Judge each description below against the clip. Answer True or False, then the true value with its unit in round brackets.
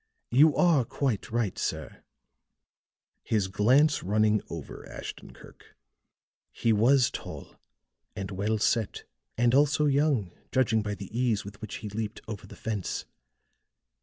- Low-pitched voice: True (110 Hz)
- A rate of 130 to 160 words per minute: True (135 wpm)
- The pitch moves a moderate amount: True (4.2 semitones)